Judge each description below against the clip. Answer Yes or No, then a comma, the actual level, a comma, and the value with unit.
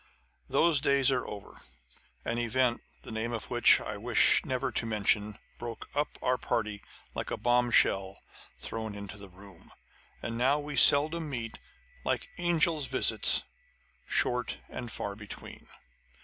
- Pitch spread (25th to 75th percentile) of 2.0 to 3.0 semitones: No, average, 4.7 semitones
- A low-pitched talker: Yes, low, 120 Hz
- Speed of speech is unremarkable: Yes, average, 145 wpm